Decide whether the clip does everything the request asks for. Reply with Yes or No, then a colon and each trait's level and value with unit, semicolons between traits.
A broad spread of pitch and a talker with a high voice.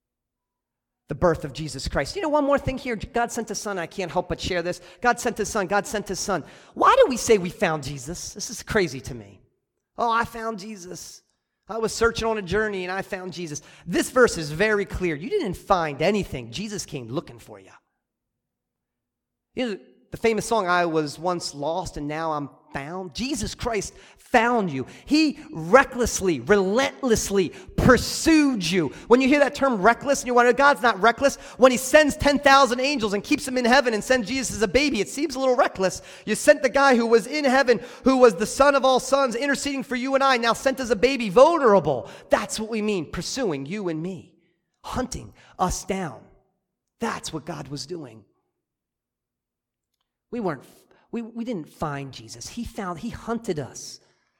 Yes: wide, 6.4 semitones; high, 215 Hz